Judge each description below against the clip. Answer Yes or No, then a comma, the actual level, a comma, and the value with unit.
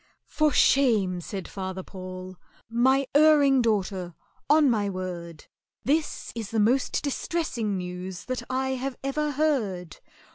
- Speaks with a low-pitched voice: No, high, 225 Hz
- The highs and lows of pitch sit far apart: Yes, wide, 6.7 semitones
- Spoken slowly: Yes, slow, 130 wpm